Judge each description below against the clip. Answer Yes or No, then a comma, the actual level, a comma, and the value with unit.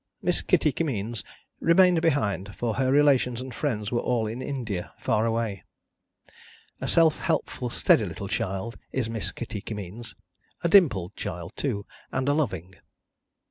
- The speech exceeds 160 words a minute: No, average, 145 wpm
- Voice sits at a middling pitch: No, low, 115 Hz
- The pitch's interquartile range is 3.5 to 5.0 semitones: No, wide, 5.4 semitones